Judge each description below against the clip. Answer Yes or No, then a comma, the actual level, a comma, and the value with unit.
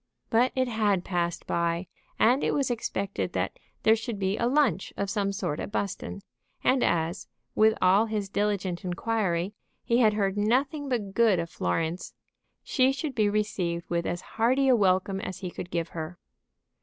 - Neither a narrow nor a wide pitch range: Yes, average, 4.4 semitones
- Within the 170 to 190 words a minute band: Yes, average, 175 wpm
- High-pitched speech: Yes, high, 205 Hz